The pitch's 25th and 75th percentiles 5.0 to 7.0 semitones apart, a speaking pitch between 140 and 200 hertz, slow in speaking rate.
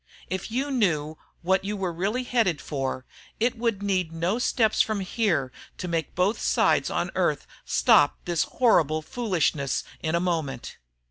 No: wide, 5.6 semitones; medium, 185 Hz; average, 155 wpm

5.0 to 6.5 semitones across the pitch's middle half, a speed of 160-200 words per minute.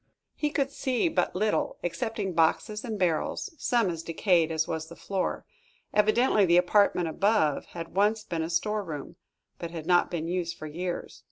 No: average, 4.3 semitones; average, 175 wpm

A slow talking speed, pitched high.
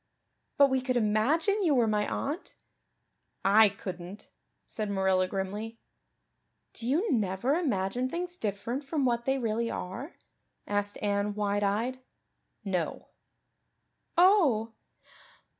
Yes: slow, 115 wpm; high, 225 Hz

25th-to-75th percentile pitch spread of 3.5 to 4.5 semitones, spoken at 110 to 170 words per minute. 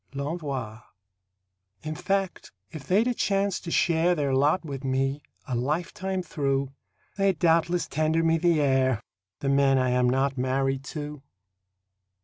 Yes: average, 4.0 semitones; average, 140 wpm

